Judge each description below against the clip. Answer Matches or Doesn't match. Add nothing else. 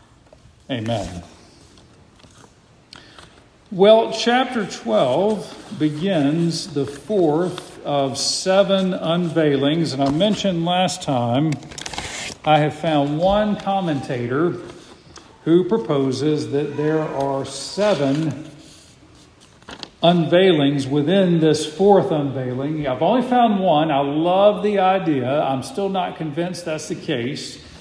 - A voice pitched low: Doesn't match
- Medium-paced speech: Doesn't match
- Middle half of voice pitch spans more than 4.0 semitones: Matches